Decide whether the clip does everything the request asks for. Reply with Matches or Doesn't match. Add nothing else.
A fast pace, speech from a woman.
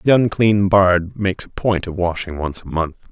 Doesn't match